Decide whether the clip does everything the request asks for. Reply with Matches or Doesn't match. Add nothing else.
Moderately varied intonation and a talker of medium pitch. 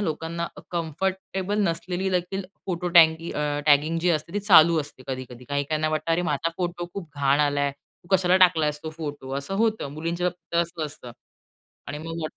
Matches